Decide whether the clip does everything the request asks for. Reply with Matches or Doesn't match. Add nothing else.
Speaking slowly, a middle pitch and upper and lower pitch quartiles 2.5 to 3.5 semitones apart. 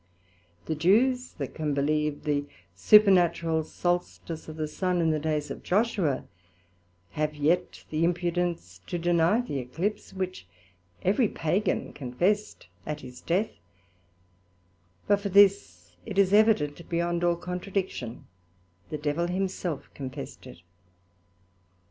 Doesn't match